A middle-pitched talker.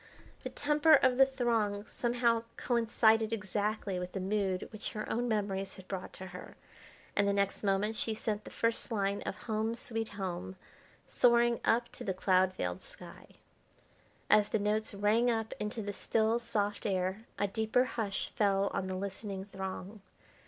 No: high, 210 Hz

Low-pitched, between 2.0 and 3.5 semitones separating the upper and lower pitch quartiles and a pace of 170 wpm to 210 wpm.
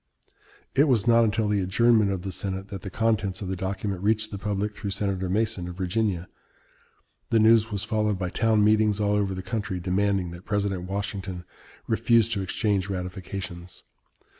Yes: low, 100 Hz; narrow, 2.5 semitones; average, 175 wpm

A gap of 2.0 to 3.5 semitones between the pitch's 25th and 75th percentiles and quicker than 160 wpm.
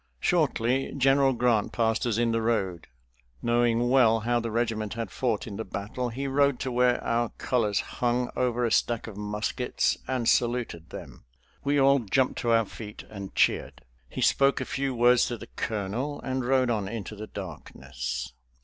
Yes: average, 2.7 semitones; average, 175 wpm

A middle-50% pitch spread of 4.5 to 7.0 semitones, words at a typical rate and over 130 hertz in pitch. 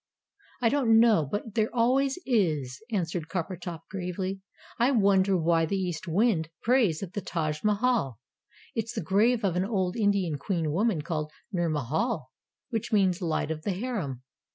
Yes: average, 5.3 semitones; average, 160 wpm; high, 190 Hz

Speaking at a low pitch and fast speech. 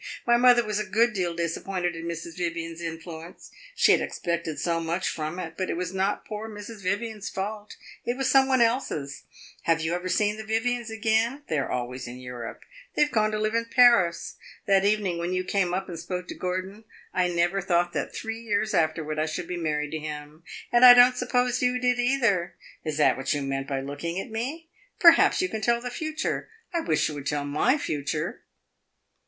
No: medium, 185 Hz; fast, 210 wpm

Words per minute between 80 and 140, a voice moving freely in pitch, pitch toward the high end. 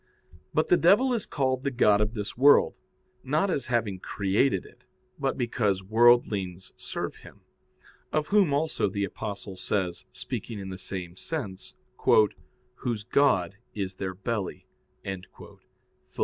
No: slow, 135 wpm; wide, 6.3 semitones; low, 105 Hz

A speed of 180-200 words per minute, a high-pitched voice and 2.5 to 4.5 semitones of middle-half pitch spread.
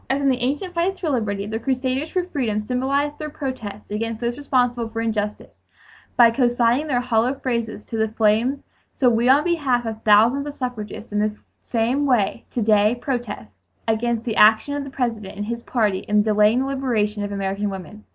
Yes: average, 190 wpm; high, 235 Hz; average, 3.9 semitones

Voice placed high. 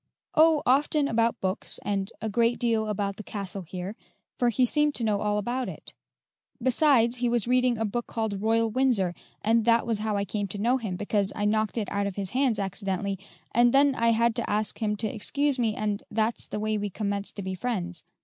Yes: high, 220 Hz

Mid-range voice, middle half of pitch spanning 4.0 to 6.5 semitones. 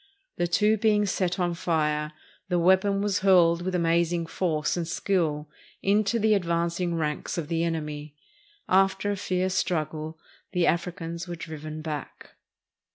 No: medium, 170 Hz; average, 2.8 semitones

